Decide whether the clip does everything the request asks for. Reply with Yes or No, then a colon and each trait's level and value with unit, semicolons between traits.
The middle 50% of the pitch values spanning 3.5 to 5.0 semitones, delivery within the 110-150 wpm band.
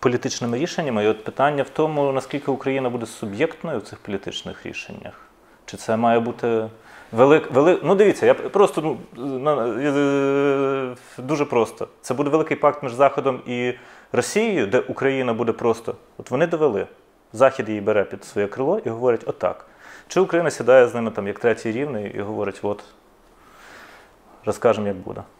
No: average, 4.2 semitones; fast, 160 wpm